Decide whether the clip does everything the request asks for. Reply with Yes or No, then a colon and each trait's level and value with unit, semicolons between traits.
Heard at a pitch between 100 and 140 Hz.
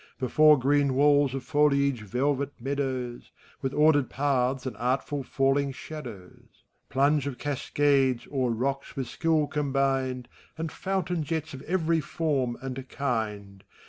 Yes: low, 135 Hz